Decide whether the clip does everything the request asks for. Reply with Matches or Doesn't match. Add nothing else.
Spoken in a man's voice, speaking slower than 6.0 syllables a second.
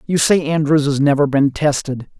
Matches